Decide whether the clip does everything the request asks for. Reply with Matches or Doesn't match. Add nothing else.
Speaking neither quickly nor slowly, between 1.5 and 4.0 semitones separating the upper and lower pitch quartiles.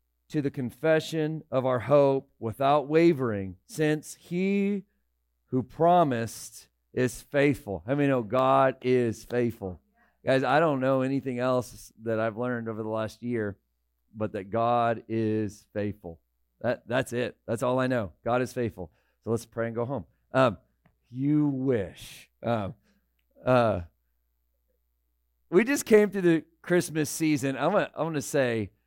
Doesn't match